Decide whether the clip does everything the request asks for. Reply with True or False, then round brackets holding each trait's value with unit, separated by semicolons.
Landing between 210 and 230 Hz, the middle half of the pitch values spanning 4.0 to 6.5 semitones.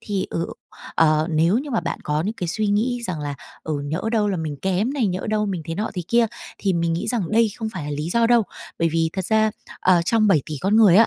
False (190 Hz; 5.0 semitones)